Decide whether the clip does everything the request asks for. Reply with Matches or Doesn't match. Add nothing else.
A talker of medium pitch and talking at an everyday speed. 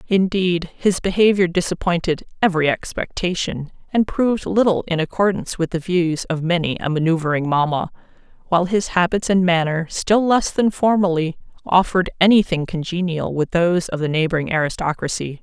Matches